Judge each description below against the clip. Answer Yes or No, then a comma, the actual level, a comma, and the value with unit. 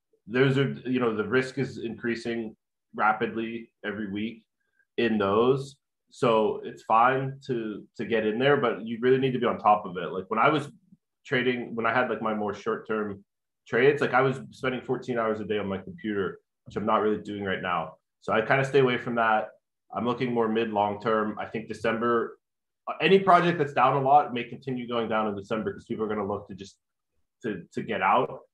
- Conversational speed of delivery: No, fast, 220 wpm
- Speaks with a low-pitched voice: Yes, low, 115 Hz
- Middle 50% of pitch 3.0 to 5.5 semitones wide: Yes, average, 3.3 semitones